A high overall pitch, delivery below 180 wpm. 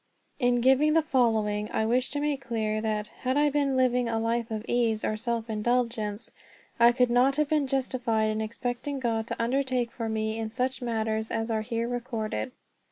No: high, 235 Hz; average, 195 wpm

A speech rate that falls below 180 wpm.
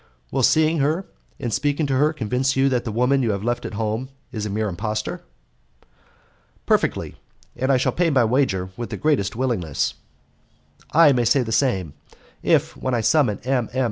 No: average, 185 wpm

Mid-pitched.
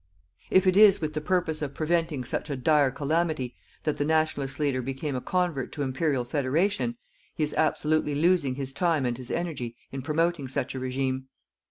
Yes: medium, 150 Hz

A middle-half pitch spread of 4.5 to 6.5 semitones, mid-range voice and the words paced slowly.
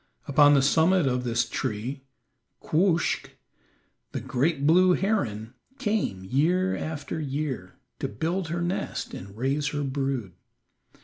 Yes: average, 5.2 semitones; medium, 145 Hz; slow, 125 wpm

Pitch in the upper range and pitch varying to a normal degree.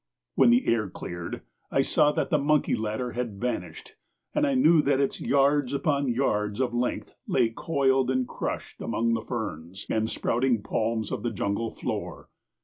No: low, 125 Hz; average, 4.1 semitones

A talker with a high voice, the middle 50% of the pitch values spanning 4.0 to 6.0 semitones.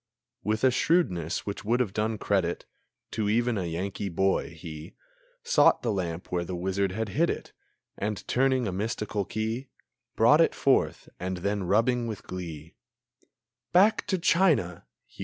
No: low, 105 Hz; average, 4.7 semitones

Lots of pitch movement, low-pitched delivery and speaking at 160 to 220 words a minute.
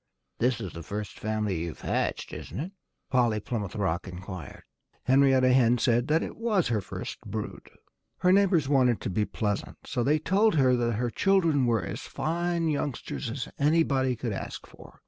Yes: wide, 6.1 semitones; low, 125 Hz; average, 175 wpm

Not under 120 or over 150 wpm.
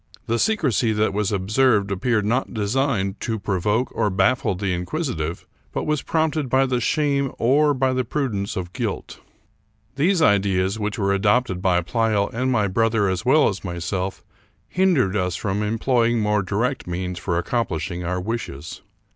No: average, 160 wpm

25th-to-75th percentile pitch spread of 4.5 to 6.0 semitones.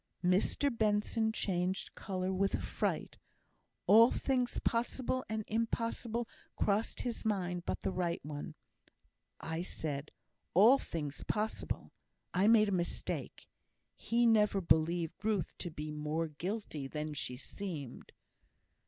Yes: average, 5.3 semitones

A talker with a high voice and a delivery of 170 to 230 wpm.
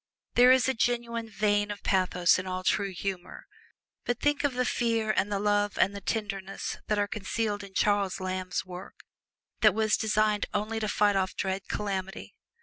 Yes: high, 205 Hz; average, 180 wpm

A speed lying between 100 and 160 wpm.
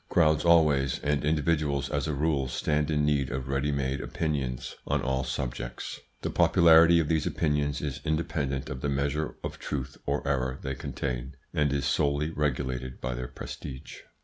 No: average, 170 wpm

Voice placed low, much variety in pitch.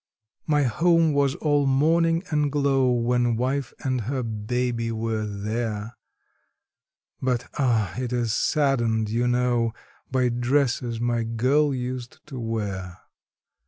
No: low, 125 Hz; average, 3.1 semitones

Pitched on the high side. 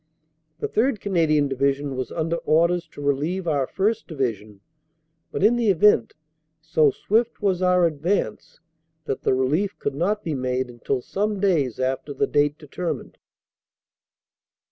No: medium, 155 Hz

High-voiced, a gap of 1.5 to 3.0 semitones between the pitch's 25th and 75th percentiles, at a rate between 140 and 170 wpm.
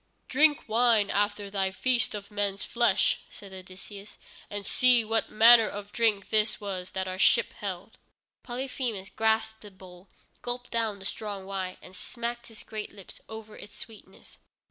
Yes: high, 210 Hz; average, 2.7 semitones; average, 160 wpm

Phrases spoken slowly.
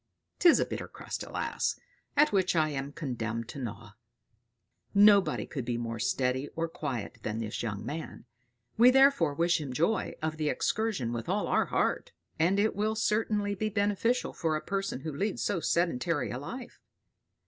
No: average, 170 wpm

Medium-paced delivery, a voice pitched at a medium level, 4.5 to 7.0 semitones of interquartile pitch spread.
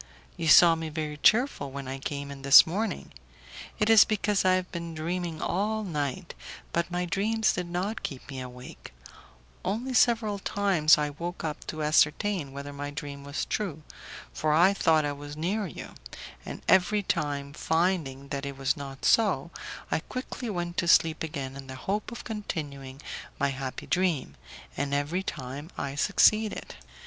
Yes: average, 170 wpm; medium, 160 Hz; average, 5.3 semitones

